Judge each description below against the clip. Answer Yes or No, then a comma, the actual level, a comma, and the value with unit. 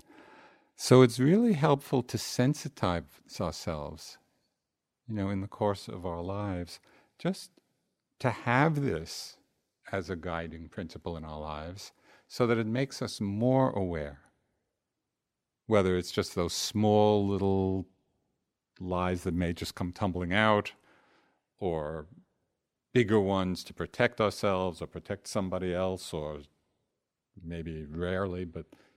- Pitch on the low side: Yes, very low, 95 Hz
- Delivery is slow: Yes, slow, 125 wpm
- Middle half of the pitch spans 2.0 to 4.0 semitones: No, average, 4.4 semitones